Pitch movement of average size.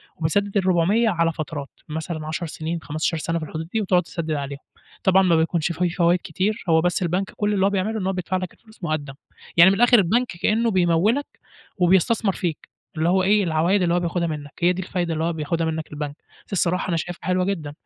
Yes: average, 3.0 semitones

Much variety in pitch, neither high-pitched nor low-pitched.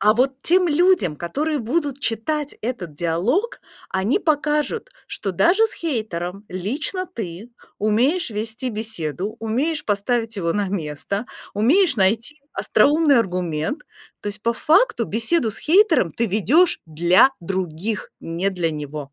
No: wide, 8.1 semitones; high, 225 Hz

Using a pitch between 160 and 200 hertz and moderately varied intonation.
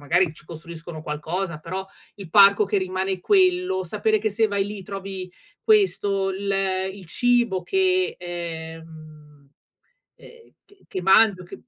Yes: high, 190 Hz; average, 3.9 semitones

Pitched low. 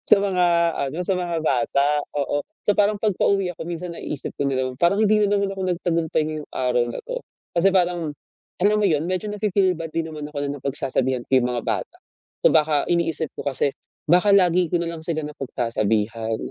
No: medium, 165 Hz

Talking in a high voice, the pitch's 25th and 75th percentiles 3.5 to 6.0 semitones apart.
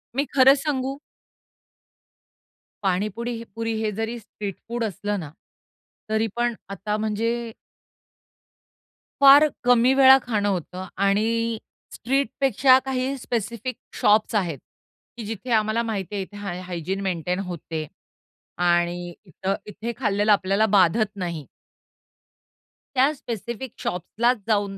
Yes: high, 215 Hz; average, 3.8 semitones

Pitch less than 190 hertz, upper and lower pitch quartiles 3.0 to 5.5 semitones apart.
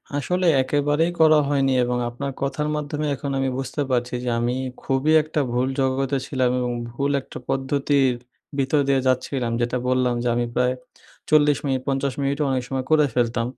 No: low, 135 Hz; narrow, 2.4 semitones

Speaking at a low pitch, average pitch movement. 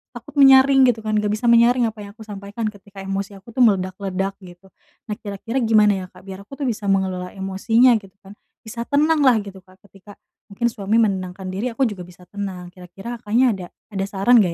No: high, 205 Hz; average, 3.4 semitones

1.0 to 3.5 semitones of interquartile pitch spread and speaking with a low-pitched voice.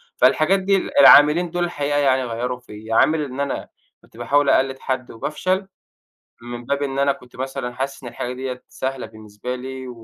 Yes: average, 2.7 semitones; low, 130 Hz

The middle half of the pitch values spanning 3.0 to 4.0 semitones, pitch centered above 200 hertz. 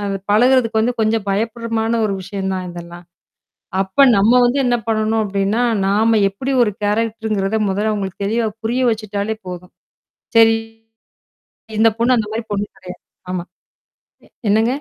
No: narrow, 2.4 semitones; high, 215 Hz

